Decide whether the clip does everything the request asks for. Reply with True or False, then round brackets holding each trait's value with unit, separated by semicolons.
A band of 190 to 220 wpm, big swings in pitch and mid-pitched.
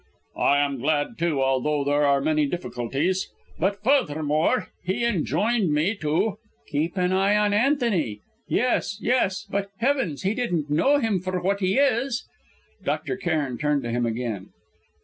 False (155 wpm; 6.3 semitones; 175 Hz)